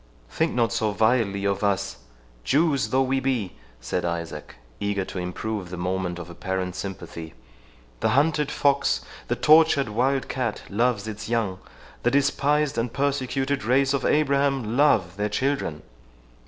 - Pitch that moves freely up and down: Yes, wide, 6.5 semitones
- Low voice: Yes, low, 115 Hz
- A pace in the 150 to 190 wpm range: No, average, 140 wpm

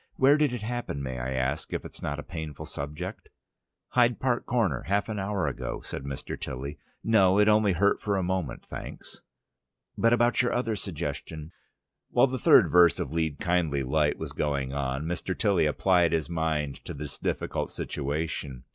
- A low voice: Yes, very low, 85 Hz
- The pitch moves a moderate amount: No, wide, 6.3 semitones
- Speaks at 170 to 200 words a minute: Yes, average, 180 wpm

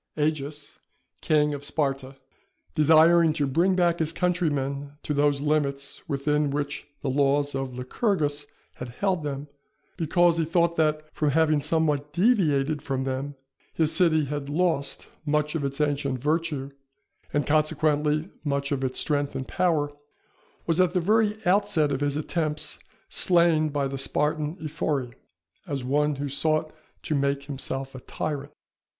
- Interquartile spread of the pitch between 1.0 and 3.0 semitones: Yes, narrow, 2.4 semitones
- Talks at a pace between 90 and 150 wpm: Yes, average, 145 wpm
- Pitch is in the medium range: Yes, medium, 150 Hz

